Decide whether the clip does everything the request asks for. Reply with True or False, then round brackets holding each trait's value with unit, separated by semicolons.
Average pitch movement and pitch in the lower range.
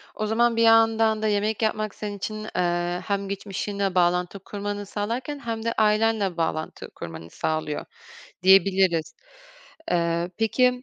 False (3.8 semitones; 205 Hz)